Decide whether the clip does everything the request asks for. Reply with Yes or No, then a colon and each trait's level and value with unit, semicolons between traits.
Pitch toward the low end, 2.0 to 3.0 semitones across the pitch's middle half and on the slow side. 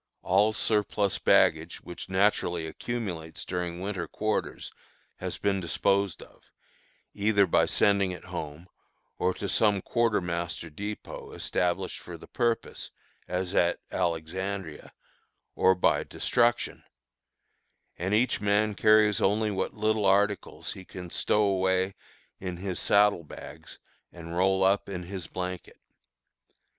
Yes: very low, 95 Hz; average, 2.7 semitones; slow, 125 wpm